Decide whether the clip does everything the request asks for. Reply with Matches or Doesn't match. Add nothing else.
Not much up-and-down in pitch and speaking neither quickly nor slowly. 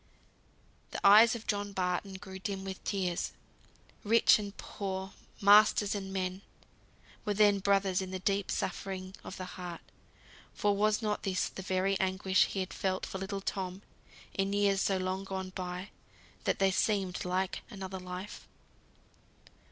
Matches